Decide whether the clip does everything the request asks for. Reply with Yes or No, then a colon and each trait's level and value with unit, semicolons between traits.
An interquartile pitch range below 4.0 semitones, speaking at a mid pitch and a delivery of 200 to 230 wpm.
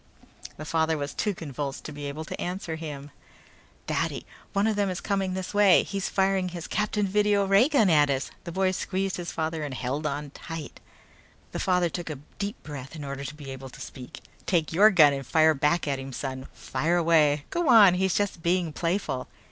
No: average, 4.8 semitones; medium, 165 Hz; fast, 205 wpm